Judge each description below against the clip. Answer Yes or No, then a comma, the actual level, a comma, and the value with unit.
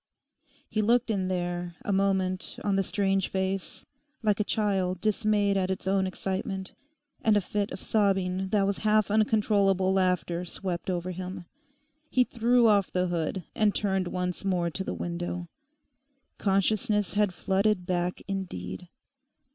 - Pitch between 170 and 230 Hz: Yes, high, 190 Hz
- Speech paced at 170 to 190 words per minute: No, average, 145 wpm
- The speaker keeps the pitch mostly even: Yes, narrow, 2.2 semitones